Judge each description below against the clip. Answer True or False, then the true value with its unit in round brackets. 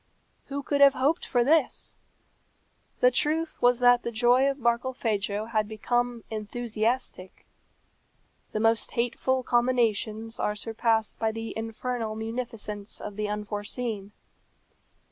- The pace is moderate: False (120 wpm)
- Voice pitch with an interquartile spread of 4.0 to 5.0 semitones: False (2.4 semitones)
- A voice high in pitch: True (230 Hz)